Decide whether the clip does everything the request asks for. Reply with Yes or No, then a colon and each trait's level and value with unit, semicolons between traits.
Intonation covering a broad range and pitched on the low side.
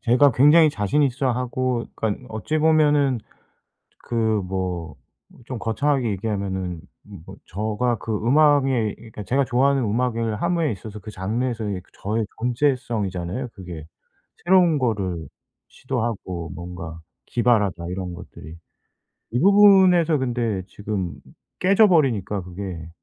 Yes: wide, 5.9 semitones; low, 115 Hz